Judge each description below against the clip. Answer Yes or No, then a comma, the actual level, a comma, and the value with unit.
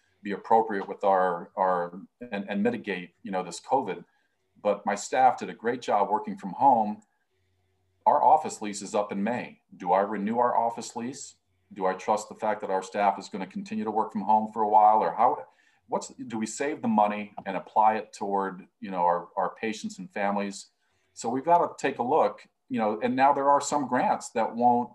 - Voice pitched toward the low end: Yes, low, 105 Hz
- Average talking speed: No, fast, 215 wpm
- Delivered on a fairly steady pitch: No, average, 3.7 semitones